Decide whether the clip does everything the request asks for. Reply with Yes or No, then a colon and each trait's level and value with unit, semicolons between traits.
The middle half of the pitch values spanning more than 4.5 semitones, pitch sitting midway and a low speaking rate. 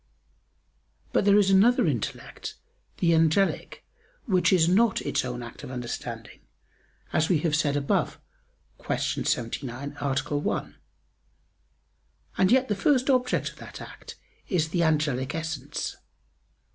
Yes: wide, 5.6 semitones; medium, 160 Hz; slow, 130 wpm